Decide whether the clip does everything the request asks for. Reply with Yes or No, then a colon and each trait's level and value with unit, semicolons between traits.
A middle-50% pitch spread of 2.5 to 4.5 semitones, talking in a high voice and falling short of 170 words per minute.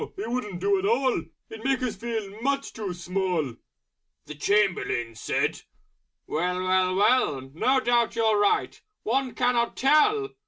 No: wide, 5.5 semitones; high, 210 Hz; average, 155 wpm